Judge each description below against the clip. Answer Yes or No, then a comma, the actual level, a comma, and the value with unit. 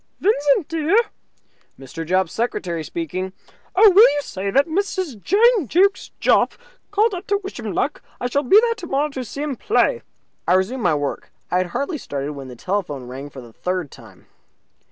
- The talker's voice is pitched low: No, very high, 260 Hz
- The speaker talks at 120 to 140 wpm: No, average, 185 wpm